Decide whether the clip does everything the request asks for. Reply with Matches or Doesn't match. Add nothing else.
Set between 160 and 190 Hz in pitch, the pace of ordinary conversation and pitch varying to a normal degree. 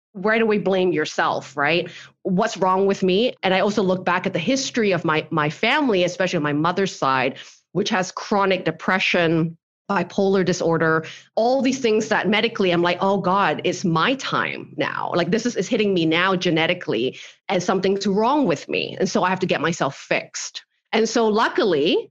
Matches